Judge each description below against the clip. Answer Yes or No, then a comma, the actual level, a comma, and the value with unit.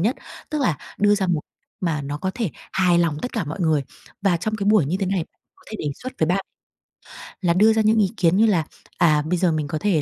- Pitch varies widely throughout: No, average, 4.4 semitones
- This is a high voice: No, medium, 180 Hz